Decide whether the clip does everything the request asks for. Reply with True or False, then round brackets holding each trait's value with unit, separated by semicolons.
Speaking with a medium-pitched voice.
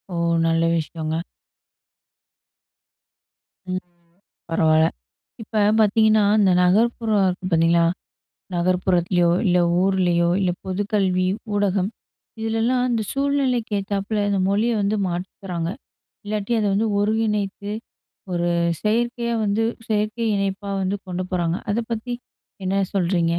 False (200 Hz)